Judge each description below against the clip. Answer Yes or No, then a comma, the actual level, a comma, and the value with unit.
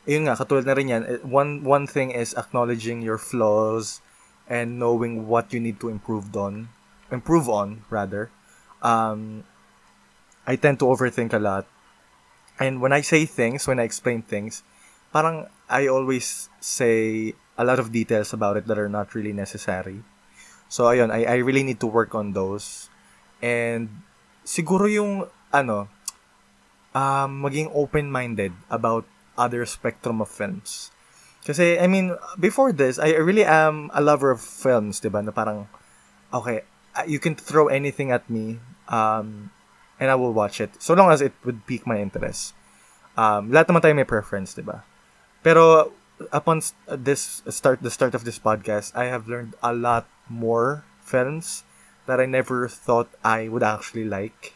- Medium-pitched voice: No, low, 120 Hz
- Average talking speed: No, fast, 160 wpm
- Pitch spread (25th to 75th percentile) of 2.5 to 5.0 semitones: Yes, average, 4.2 semitones